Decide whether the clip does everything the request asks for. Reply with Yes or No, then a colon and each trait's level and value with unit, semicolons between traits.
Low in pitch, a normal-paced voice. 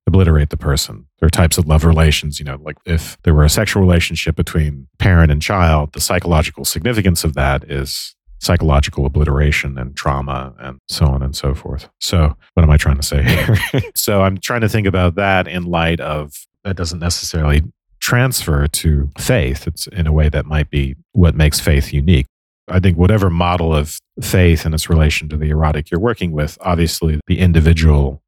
Yes: very low, 80 Hz; average, 195 wpm